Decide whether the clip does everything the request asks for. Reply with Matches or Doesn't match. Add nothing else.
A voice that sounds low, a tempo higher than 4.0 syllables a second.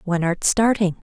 Doesn't match